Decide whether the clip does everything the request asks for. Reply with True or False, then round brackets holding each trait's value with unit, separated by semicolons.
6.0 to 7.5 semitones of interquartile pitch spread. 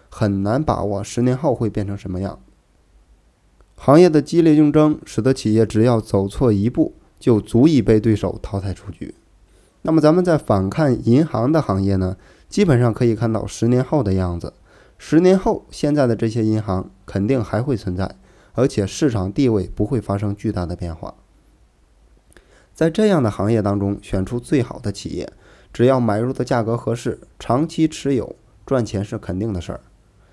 False (5.2 semitones)